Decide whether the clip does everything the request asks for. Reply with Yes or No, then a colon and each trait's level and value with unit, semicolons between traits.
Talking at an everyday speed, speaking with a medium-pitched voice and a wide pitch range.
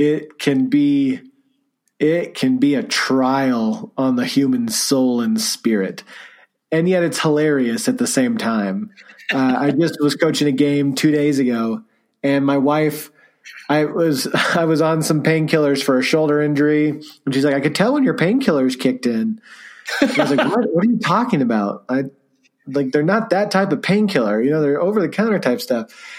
Yes: average, 190 wpm; medium, 155 Hz; wide, 7.5 semitones